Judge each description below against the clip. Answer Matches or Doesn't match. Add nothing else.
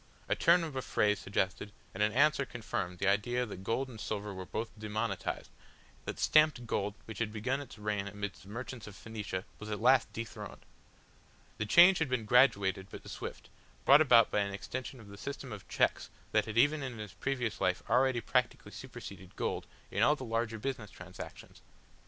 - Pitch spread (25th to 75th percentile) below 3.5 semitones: Doesn't match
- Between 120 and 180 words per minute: Doesn't match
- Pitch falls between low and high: Doesn't match